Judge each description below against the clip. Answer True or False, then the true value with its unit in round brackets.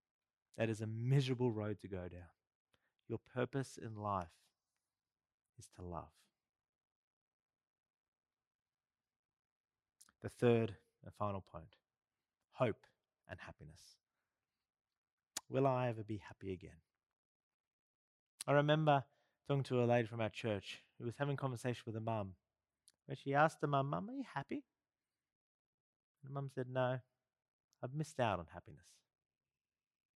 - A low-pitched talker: True (115 Hz)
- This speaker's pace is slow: True (130 wpm)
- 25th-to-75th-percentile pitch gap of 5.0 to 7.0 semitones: True (5.3 semitones)